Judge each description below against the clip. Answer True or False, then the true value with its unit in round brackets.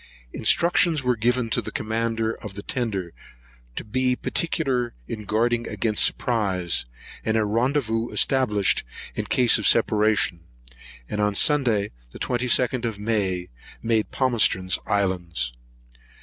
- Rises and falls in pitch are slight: False (3.2 semitones)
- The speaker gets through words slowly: True (125 wpm)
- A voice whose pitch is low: True (115 Hz)